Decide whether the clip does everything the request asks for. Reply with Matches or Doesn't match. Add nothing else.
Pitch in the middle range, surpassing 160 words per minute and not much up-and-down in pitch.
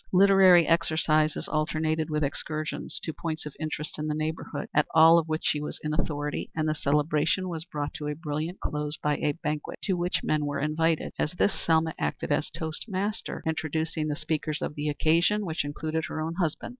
Matches